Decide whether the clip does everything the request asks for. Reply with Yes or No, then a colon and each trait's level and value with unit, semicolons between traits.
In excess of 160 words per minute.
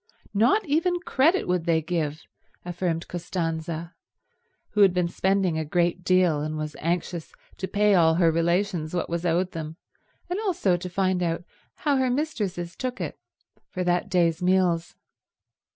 No: average, 155 wpm